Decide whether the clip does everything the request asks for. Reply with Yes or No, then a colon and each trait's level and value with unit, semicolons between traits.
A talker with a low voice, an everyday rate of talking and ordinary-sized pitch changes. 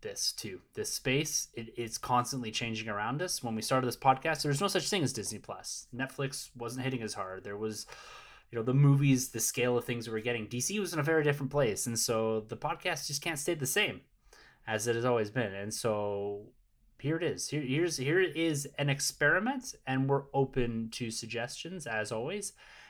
No: low, 130 Hz; fast, 210 wpm; average, 4.1 semitones